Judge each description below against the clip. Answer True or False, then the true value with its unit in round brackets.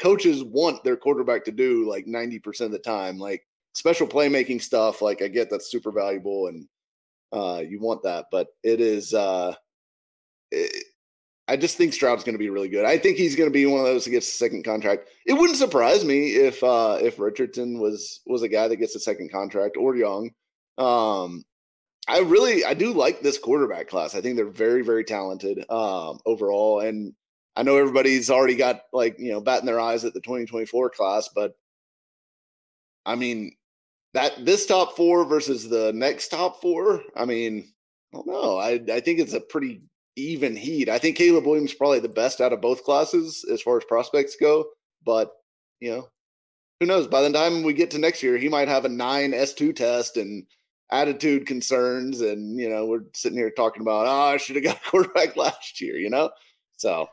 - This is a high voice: False (135 Hz)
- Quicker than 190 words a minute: True (200 wpm)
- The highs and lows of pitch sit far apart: True (8.1 semitones)